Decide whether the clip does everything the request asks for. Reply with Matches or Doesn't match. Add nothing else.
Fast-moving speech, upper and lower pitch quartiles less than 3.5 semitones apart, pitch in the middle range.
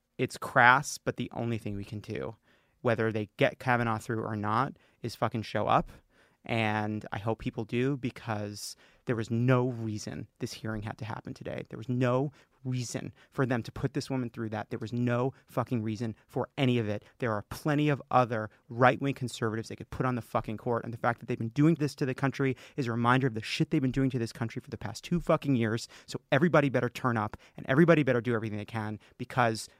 Doesn't match